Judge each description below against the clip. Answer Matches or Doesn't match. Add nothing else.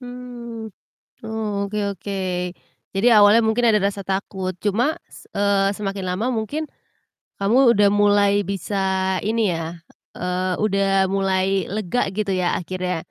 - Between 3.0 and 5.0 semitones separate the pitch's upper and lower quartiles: Doesn't match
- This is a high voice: Matches